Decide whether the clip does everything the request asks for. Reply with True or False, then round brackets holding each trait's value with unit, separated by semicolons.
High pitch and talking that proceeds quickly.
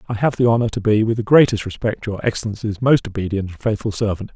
False (110 Hz; 235 wpm)